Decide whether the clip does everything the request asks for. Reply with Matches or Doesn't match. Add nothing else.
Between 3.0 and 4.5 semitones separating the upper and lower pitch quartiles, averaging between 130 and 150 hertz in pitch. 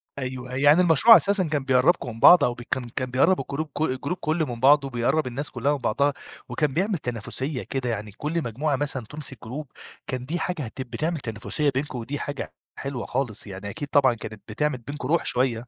Matches